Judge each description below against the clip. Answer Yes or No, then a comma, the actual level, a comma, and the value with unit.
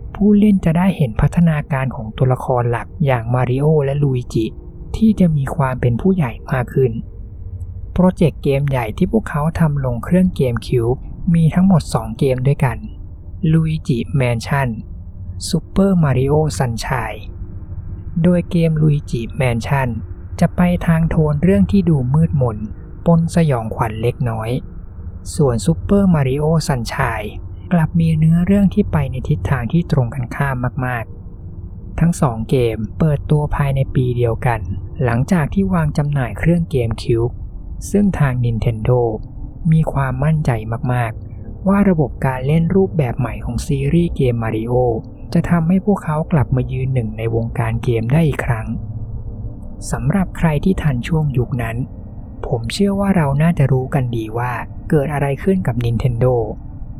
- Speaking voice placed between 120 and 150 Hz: Yes, low, 130 Hz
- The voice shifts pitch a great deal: Yes, wide, 5.8 semitones